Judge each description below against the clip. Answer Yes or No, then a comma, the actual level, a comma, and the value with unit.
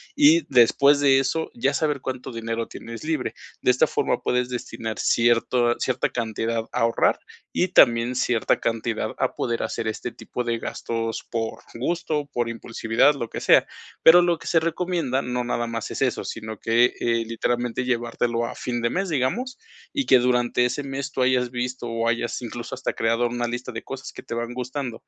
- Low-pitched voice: Yes, low, 120 Hz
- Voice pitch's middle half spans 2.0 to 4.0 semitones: Yes, narrow, 2.5 semitones